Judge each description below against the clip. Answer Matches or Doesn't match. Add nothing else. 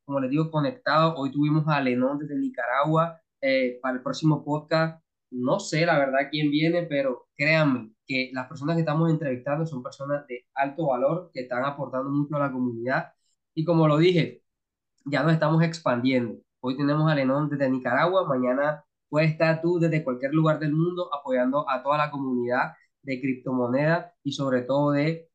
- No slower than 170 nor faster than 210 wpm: Matches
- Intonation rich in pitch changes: Doesn't match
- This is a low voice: Doesn't match